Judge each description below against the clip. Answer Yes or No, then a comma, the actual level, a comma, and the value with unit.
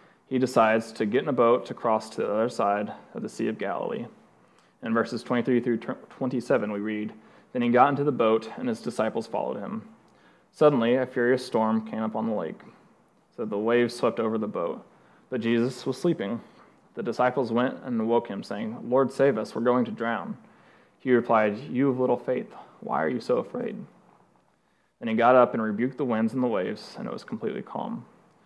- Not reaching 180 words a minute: No, fast, 205 wpm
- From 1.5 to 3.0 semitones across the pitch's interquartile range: Yes, narrow, 2.4 semitones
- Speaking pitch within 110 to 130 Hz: Yes, low, 120 Hz